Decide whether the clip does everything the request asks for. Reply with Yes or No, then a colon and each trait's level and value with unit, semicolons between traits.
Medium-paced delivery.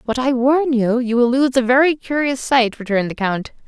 No: fast, 230 wpm